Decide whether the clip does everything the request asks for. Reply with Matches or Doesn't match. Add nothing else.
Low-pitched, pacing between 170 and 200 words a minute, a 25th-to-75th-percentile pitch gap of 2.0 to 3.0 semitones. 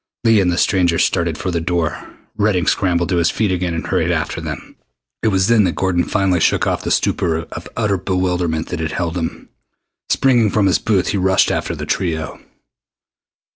Matches